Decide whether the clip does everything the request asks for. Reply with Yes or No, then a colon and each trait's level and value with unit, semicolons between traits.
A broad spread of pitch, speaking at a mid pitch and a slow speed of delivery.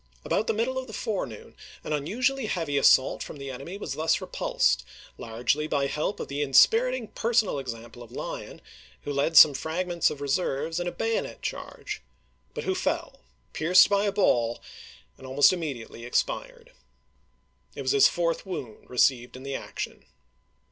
No: wide, 7.5 semitones; medium, 155 Hz; average, 165 wpm